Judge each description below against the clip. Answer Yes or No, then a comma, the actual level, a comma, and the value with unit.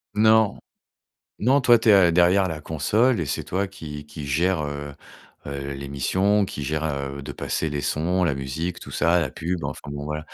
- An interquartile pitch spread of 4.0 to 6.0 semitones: Yes, average, 4.7 semitones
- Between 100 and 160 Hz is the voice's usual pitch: No, very low, 80 Hz